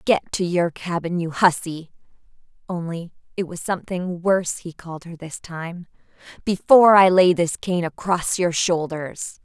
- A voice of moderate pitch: Yes, medium, 175 Hz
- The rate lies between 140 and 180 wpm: Yes, average, 155 wpm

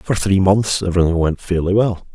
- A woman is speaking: No, male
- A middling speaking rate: Yes, average, 195 wpm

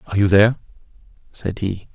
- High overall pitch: No, low, 100 Hz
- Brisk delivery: No, average, 155 wpm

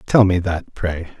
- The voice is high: No, very low, 90 Hz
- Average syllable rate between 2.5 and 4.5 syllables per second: Yes, 4.0 syllables/s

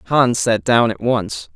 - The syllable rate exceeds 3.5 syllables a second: No, 3.4 syllables/s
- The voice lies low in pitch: Yes, low, 115 Hz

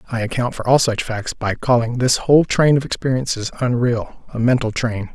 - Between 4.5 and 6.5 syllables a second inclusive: Yes, 5.3 syllables/s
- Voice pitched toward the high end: No, low, 120 Hz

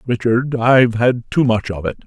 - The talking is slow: No, fast, 205 wpm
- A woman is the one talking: No, male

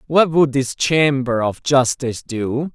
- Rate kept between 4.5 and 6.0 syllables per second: No, 3.9 syllables/s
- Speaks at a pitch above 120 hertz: Yes, low, 135 Hz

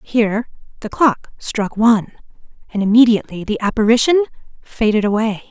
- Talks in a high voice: Yes, high, 220 Hz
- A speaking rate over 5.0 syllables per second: Yes, 5.8 syllables/s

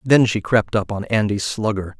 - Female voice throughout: No, male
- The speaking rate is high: Yes, fast, 210 wpm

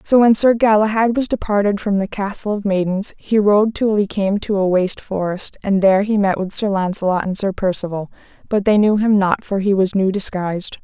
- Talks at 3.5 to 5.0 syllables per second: No, 5.5 syllables/s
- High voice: Yes, high, 200 Hz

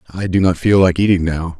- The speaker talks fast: Yes, fast, 265 wpm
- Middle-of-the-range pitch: No, very low, 90 Hz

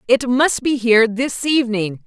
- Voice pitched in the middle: No, high, 245 Hz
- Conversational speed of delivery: Yes, average, 175 wpm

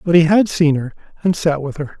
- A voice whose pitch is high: No, medium, 160 Hz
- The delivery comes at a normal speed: No, fast, 270 wpm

